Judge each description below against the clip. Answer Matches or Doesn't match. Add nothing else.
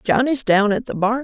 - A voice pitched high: Matches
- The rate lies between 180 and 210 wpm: Doesn't match